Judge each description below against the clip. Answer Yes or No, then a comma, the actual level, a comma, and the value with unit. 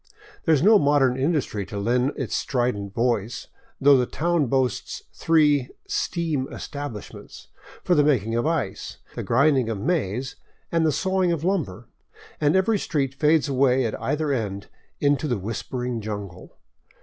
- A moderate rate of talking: Yes, average, 160 wpm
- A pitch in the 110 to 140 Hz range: Yes, low, 135 Hz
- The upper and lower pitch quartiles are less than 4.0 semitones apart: No, average, 4.8 semitones